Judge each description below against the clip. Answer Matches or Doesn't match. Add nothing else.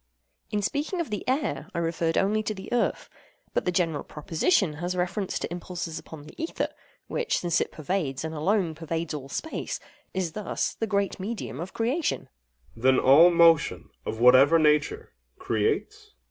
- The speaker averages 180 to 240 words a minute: Doesn't match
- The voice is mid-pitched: Matches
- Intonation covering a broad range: Doesn't match